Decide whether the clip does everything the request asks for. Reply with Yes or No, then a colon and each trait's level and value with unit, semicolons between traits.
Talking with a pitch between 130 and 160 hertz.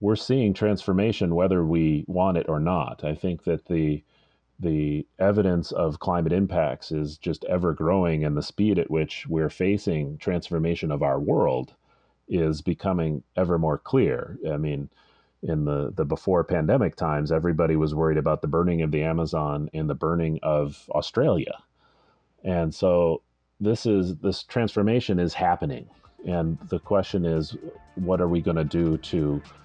No: very low, 80 Hz